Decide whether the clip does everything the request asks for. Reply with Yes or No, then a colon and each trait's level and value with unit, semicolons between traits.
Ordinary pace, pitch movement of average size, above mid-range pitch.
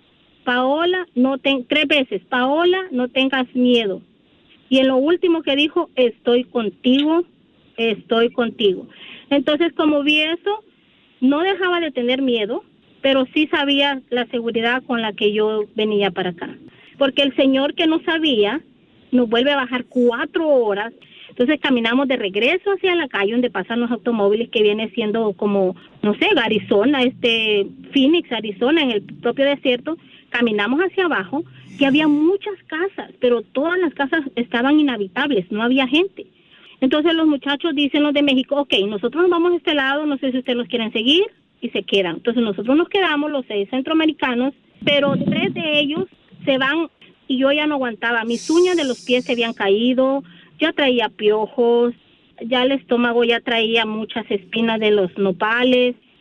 Yes: average, 165 wpm; average, 4.3 semitones; very high, 260 Hz